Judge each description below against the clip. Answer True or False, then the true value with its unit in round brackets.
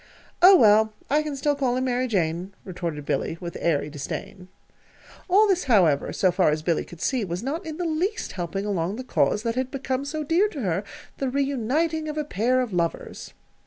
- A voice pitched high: True (245 Hz)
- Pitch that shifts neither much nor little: False (8.6 semitones)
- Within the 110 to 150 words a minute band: False (200 wpm)